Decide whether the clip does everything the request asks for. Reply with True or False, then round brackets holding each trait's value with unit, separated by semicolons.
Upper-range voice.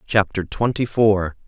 False (100 Hz)